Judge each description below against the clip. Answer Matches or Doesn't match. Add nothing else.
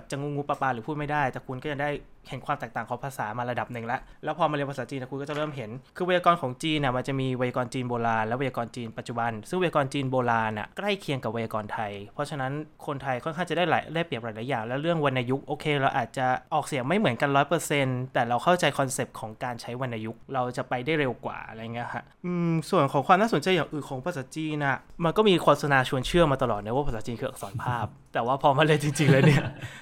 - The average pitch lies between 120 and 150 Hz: Matches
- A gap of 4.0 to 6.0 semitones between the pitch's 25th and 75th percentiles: Doesn't match